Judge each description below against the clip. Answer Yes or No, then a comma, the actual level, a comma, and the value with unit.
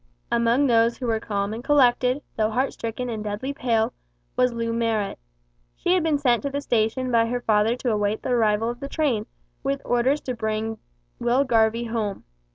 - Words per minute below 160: No, average, 190 wpm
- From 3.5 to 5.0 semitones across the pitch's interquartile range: No, narrow, 2.4 semitones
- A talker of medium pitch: No, high, 235 Hz